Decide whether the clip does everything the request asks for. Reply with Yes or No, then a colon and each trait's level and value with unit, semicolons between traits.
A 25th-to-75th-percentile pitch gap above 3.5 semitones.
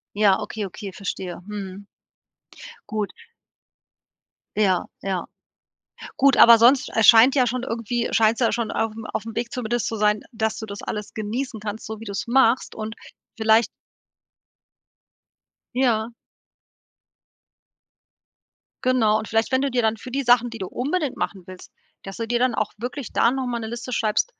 No: narrow, 2.6 semitones